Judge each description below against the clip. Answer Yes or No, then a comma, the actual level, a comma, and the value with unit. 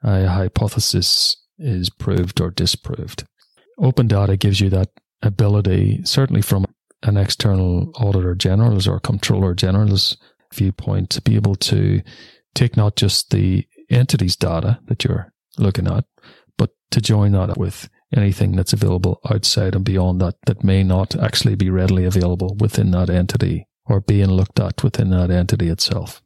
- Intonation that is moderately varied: Yes, average, 3.5 semitones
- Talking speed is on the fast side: No, average, 150 wpm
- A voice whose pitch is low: Yes, low, 100 Hz